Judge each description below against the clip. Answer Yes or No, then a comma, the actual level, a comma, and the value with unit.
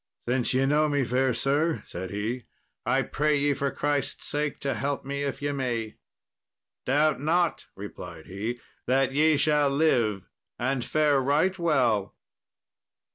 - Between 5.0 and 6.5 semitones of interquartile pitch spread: No, average, 3.3 semitones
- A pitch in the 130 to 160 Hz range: Yes, medium, 140 Hz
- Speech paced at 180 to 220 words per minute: No, average, 145 wpm